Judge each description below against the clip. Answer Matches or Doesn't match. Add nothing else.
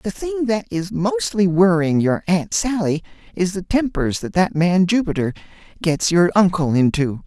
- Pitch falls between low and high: Matches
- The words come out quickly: Doesn't match